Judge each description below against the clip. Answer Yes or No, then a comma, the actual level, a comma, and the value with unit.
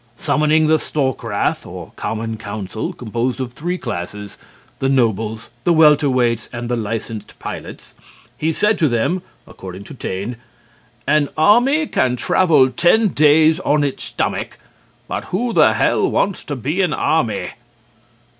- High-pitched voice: No, low, 135 Hz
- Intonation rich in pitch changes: Yes, wide, 5.7 semitones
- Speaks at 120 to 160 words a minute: Yes, average, 140 wpm